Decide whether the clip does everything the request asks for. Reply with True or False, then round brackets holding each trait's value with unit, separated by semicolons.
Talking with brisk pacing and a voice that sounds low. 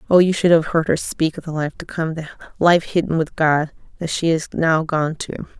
False (235 wpm; 160 Hz)